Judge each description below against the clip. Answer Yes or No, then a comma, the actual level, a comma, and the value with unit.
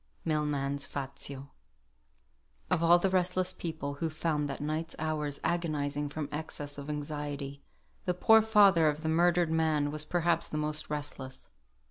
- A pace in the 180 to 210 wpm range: No, average, 145 wpm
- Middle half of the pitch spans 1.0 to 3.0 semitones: Yes, narrow, 2.6 semitones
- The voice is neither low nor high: Yes, medium, 155 Hz